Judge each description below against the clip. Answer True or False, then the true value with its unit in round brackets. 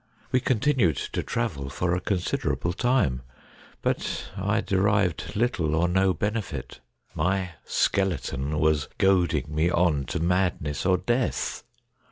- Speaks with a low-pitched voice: True (90 Hz)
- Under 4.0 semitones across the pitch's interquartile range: False (4.5 semitones)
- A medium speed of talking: False (125 wpm)